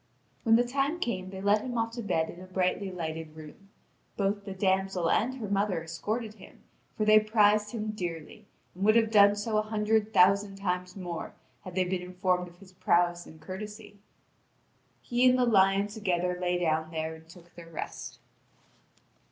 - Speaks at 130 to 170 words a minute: No, average, 185 wpm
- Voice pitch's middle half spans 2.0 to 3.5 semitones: Yes, average, 3.2 semitones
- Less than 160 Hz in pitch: No, high, 195 Hz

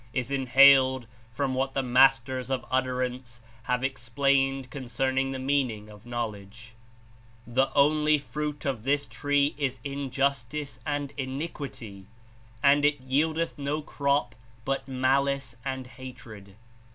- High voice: No, low, 135 Hz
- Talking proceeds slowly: Yes, slow, 125 wpm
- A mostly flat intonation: Yes, narrow, 2.0 semitones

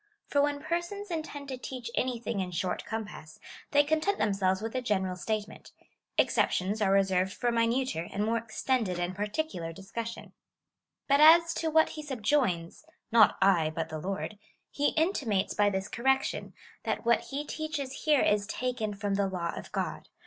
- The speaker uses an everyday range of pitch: No, wide, 6.6 semitones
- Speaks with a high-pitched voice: Yes, high, 225 Hz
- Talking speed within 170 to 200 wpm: Yes, average, 180 wpm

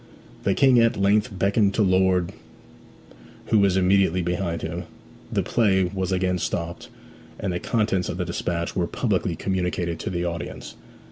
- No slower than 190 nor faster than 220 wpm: No, average, 155 wpm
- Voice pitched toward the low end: Yes, very low, 95 Hz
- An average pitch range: No, narrow, 2.1 semitones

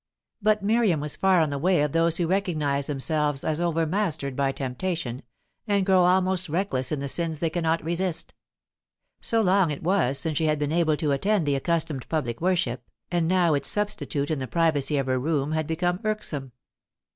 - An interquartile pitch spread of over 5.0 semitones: No, average, 4.1 semitones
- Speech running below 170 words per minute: No, average, 190 wpm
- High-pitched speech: No, medium, 160 Hz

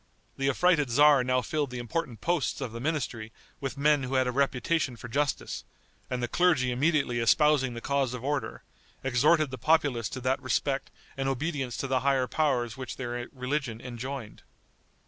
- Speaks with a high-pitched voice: No, low, 130 Hz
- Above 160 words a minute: Yes, average, 175 wpm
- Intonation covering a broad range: No, average, 3.0 semitones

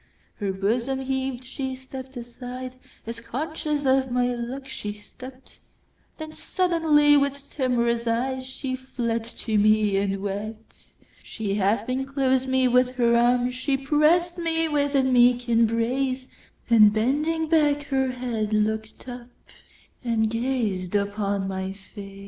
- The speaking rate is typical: No, slow, 115 wpm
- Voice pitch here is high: Yes, very high, 250 Hz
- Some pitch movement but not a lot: Yes, average, 3.2 semitones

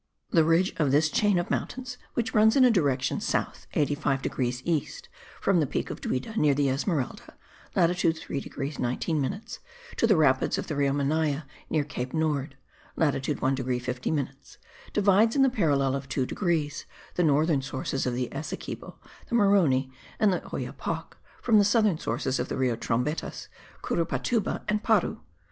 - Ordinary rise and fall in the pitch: No, wide, 5.8 semitones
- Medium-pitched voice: Yes, medium, 150 Hz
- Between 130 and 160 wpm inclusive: No, average, 170 wpm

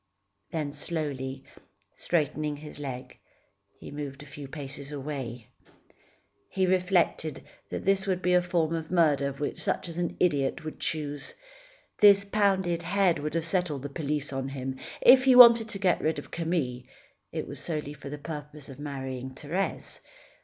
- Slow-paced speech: No, average, 160 wpm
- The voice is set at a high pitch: No, medium, 150 Hz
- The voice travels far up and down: No, average, 4.1 semitones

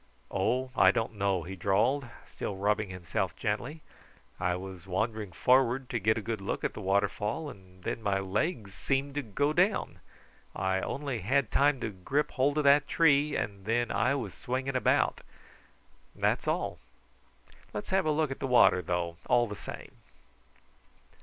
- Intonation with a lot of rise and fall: Yes, wide, 6.0 semitones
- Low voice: Yes, low, 115 Hz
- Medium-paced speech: Yes, average, 165 wpm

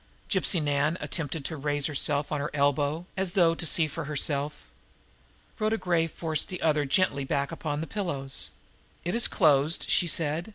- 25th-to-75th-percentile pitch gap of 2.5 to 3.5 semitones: Yes, average, 3.1 semitones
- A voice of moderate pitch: Yes, medium, 155 Hz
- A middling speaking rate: Yes, average, 170 wpm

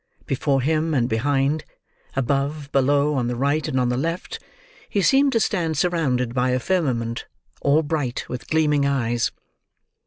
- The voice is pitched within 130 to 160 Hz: Yes, medium, 140 Hz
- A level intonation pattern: No, average, 3.8 semitones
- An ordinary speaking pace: Yes, average, 155 wpm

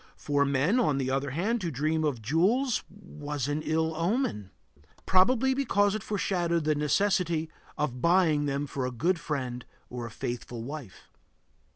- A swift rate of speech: No, average, 160 wpm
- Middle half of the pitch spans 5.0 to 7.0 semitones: Yes, wide, 5.4 semitones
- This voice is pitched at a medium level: Yes, medium, 155 Hz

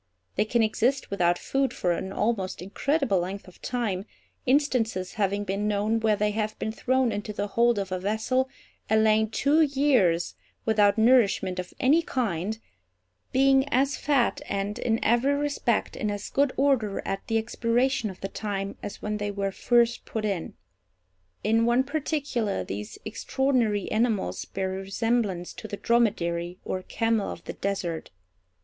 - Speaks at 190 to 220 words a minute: No, average, 160 wpm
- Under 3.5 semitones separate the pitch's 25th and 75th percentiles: No, average, 3.9 semitones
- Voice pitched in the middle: No, high, 215 Hz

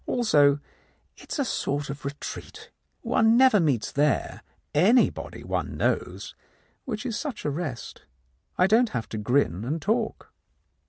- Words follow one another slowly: No, average, 145 wpm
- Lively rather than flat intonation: Yes, wide, 8.6 semitones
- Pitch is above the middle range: No, medium, 170 Hz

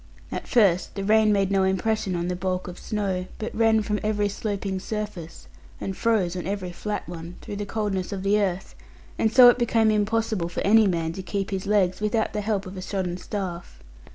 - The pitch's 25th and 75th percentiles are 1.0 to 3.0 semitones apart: Yes, narrow, 2.5 semitones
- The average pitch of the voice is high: Yes, high, 200 Hz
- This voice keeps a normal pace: No, fast, 210 wpm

